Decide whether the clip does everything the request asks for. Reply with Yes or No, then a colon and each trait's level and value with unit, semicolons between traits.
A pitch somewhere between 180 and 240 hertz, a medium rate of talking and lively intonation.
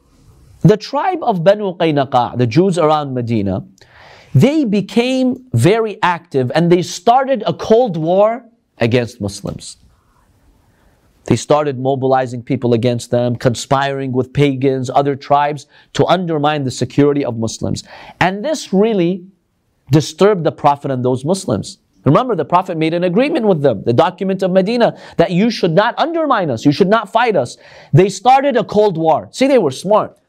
No: medium, 160 Hz; average, 155 wpm; wide, 7.6 semitones